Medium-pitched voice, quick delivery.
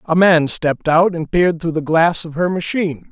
Yes: medium, 165 Hz; fast, 230 wpm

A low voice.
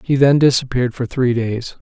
Yes: low, 125 Hz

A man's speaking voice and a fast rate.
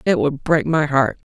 Yes: male; fast, 230 wpm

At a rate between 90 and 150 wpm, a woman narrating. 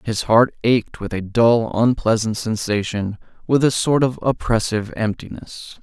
No: average, 145 wpm; male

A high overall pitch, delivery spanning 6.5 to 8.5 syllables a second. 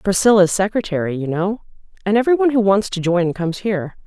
Yes: high, 195 Hz; 6.7 syllables/s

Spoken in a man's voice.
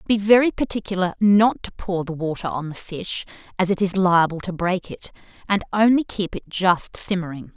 No: female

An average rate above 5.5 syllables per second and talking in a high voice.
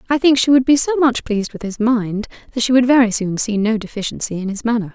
Yes: 6.3 syllables/s; high, 235 Hz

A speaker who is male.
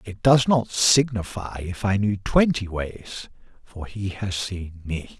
Yes: male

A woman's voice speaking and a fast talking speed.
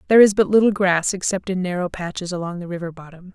Yes: female; fast, 235 wpm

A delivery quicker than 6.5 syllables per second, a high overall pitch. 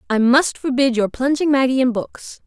No: 4.9 syllables/s; very high, 255 Hz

